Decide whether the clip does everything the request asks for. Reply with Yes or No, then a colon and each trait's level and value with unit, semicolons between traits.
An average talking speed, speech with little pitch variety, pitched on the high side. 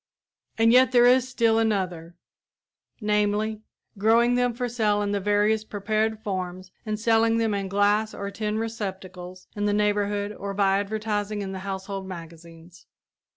Yes: average, 155 wpm; narrow, 2.2 semitones; high, 205 Hz